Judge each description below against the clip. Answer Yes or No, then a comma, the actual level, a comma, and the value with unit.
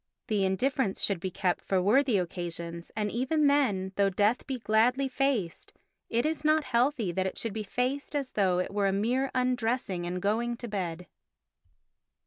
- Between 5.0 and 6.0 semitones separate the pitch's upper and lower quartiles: Yes, average, 5.3 semitones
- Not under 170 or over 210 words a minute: Yes, average, 175 wpm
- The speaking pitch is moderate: No, high, 220 Hz